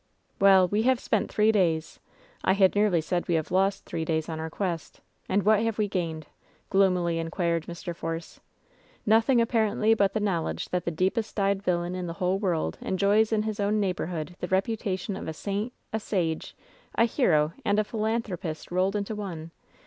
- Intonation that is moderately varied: Yes, average, 3.8 semitones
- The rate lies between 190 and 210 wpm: Yes, average, 195 wpm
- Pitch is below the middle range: No, high, 190 Hz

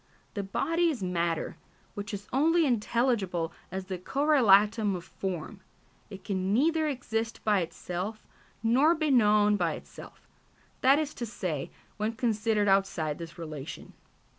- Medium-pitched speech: No, high, 210 Hz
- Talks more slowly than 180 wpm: Yes, average, 140 wpm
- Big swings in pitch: No, average, 5.0 semitones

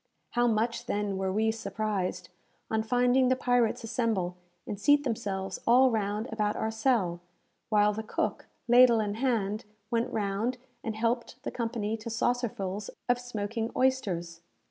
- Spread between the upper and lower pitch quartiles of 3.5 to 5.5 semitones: No, average, 2.8 semitones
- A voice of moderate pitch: No, high, 220 Hz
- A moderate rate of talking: Yes, average, 145 wpm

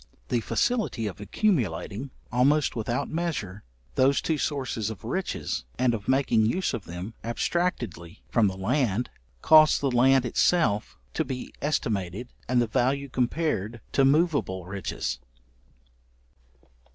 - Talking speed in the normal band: No, slow, 125 wpm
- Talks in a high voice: No, low, 120 Hz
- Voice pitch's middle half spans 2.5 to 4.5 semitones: No, wide, 5.4 semitones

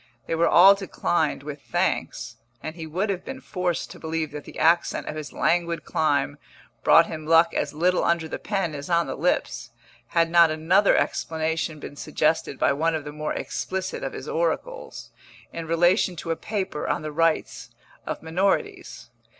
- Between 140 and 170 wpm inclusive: No, average, 180 wpm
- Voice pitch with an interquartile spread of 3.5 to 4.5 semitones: No, narrow, 2.4 semitones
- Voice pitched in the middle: Yes, medium, 165 Hz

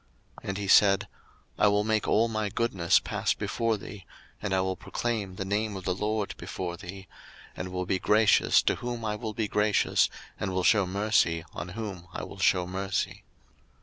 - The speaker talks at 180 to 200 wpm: Yes, average, 190 wpm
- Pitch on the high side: No, low, 100 Hz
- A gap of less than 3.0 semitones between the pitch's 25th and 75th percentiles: Yes, narrow, 2.4 semitones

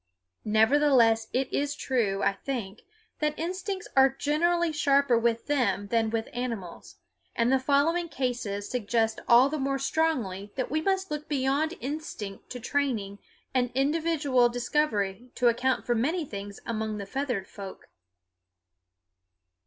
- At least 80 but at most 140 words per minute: Yes, slow, 135 wpm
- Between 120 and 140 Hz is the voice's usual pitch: No, very high, 255 Hz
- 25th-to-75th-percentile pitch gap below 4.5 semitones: No, average, 4.8 semitones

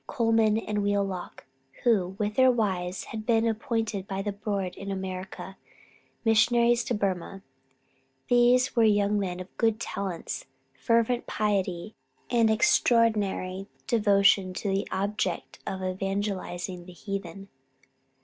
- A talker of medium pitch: No, high, 205 Hz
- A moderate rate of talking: No, slow, 120 wpm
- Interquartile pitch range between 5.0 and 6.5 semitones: No, average, 2.8 semitones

